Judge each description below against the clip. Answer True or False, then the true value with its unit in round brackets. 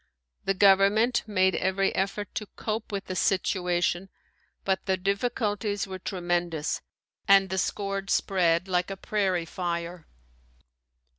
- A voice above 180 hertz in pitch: True (190 Hz)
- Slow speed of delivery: True (125 wpm)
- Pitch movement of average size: False (1.8 semitones)